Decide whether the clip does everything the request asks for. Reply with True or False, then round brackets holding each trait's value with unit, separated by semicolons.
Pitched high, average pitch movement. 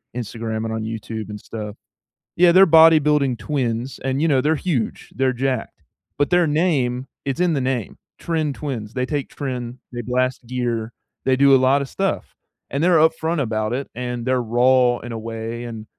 False (130 Hz; 4.0 semitones)